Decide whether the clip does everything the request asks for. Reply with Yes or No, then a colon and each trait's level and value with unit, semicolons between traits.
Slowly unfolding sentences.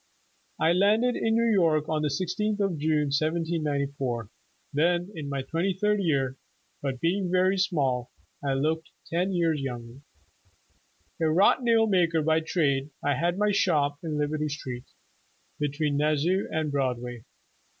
No: average, 150 wpm